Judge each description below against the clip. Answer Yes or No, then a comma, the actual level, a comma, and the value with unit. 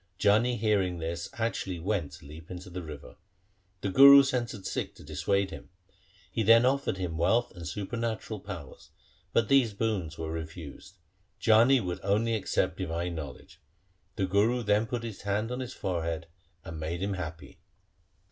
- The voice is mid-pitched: No, low, 100 Hz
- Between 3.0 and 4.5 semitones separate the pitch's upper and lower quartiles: No, average, 5.2 semitones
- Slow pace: No, average, 165 wpm